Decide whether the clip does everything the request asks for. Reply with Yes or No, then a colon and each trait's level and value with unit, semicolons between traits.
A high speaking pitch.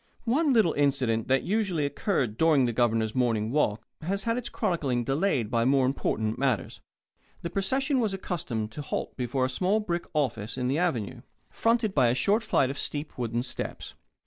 No: medium, 140 Hz